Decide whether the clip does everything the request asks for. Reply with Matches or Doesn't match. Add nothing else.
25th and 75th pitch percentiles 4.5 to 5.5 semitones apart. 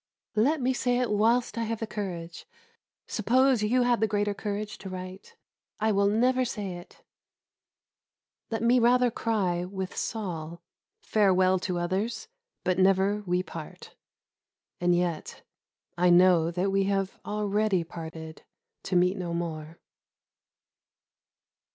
Doesn't match